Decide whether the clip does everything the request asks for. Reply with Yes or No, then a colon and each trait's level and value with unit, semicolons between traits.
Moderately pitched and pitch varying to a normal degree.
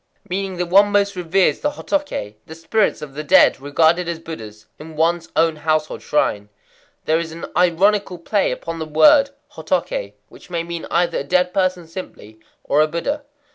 Yes: medium, 170 Hz; average, 3.2 semitones